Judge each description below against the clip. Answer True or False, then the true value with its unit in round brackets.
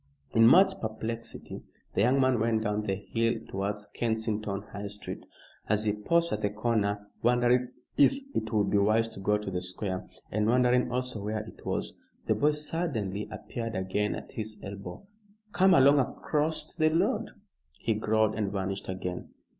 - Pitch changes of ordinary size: True (3.2 semitones)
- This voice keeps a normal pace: True (170 wpm)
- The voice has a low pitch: True (110 Hz)